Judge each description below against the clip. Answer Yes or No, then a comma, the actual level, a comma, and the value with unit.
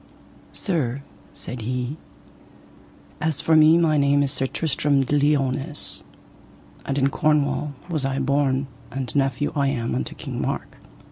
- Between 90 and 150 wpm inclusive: Yes, average, 140 wpm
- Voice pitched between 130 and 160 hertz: Yes, medium, 140 Hz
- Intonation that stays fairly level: Yes, narrow, 2.1 semitones